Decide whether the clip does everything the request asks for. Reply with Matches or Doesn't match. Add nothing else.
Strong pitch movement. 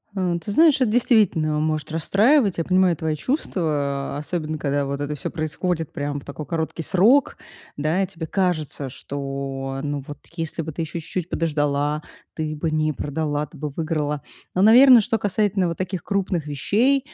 Doesn't match